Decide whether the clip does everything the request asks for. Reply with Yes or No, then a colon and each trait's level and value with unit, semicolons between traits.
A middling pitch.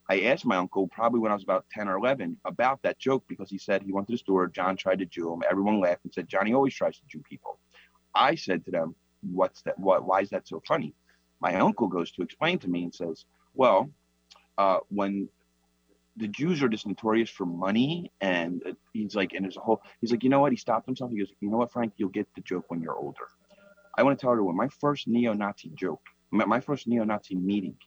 No: low, 105 Hz